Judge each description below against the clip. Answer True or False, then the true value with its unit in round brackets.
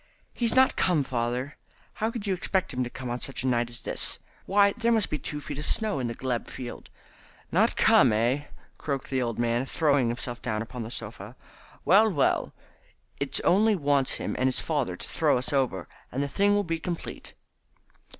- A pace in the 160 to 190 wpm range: False (200 wpm)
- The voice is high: False (135 Hz)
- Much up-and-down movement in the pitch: True (7.3 semitones)